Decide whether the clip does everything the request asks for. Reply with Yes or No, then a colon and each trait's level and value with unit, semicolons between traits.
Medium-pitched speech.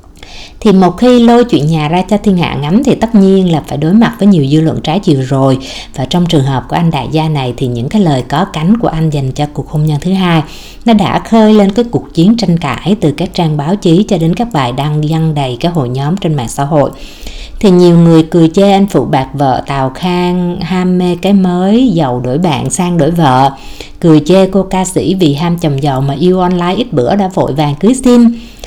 Yes: medium, 170 Hz